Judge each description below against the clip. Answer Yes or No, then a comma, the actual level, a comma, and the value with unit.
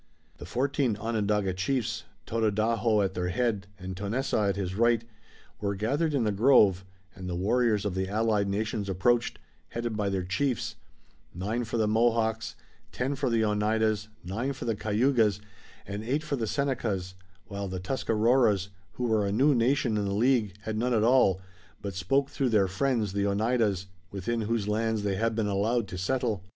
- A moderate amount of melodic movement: Yes, average, 3.1 semitones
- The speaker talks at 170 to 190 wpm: Yes, average, 175 wpm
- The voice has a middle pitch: No, low, 110 Hz